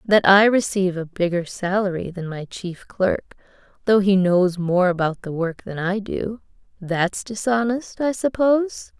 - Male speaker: No, female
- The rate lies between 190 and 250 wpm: No, average, 155 wpm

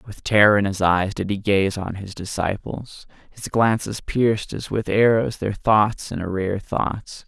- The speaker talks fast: No, average, 180 wpm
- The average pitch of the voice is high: No, low, 100 Hz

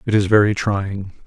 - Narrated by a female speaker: No, male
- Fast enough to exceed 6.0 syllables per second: No, 4.8 syllables/s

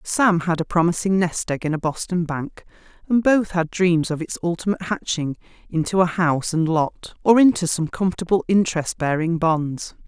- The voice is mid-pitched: Yes, medium, 175 Hz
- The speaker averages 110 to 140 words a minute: No, average, 180 wpm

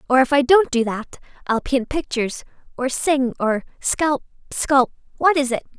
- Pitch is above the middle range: Yes, very high, 265 Hz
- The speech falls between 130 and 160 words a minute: Yes, average, 155 wpm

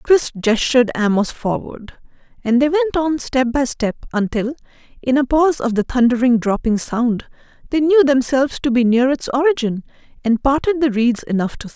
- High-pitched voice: Yes, very high, 255 Hz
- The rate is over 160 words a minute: Yes, average, 180 wpm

